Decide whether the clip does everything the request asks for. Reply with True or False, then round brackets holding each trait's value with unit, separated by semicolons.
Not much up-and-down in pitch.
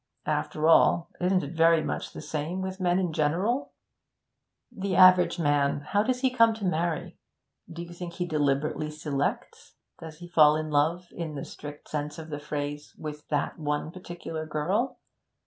False (3.2 semitones)